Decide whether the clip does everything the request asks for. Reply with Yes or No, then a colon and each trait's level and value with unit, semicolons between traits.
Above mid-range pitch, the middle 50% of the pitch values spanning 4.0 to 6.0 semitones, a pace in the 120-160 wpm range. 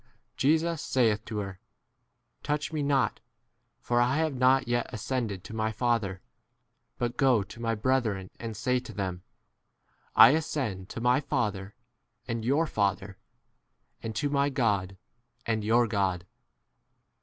No: low, 115 Hz; average, 4.3 semitones; average, 145 wpm